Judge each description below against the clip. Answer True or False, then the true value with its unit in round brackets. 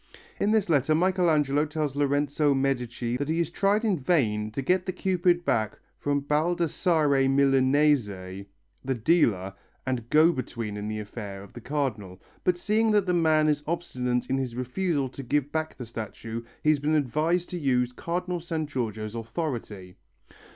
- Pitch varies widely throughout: True (5.8 semitones)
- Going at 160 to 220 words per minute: True (165 wpm)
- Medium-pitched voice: True (145 Hz)